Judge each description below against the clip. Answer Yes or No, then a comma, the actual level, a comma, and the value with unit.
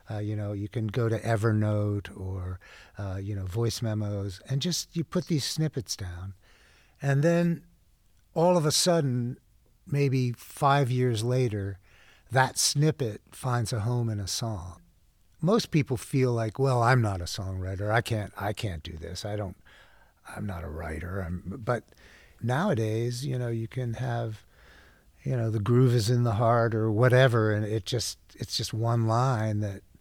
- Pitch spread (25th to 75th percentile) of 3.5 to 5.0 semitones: Yes, average, 4.2 semitones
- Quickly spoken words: No, average, 170 wpm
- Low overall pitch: Yes, low, 115 Hz